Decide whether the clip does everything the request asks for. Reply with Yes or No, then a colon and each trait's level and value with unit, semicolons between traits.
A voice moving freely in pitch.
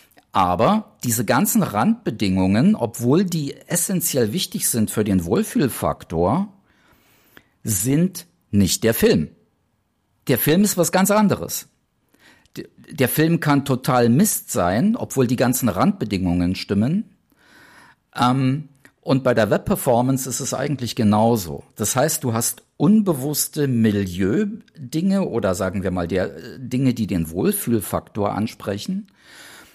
Yes: wide, 8.2 semitones